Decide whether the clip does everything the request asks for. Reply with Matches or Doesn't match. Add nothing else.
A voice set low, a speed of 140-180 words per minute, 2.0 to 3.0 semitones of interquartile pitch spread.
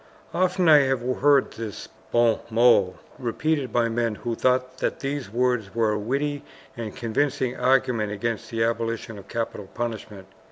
Matches